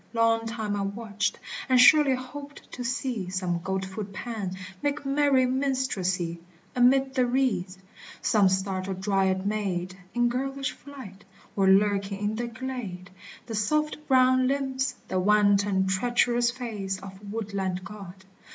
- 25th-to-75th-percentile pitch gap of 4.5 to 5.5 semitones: Yes, average, 5.0 semitones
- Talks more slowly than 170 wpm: Yes, slow, 135 wpm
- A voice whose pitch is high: Yes, high, 215 Hz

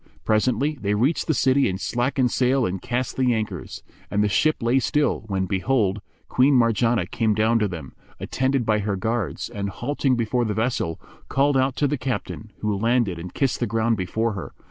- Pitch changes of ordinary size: Yes, average, 4.0 semitones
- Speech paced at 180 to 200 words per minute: Yes, average, 190 wpm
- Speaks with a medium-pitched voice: No, low, 115 Hz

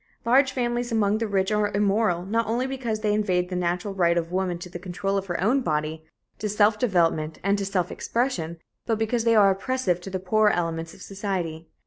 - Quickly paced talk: Yes, fast, 210 wpm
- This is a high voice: Yes, high, 195 Hz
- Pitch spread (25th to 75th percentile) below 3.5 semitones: No, average, 3.9 semitones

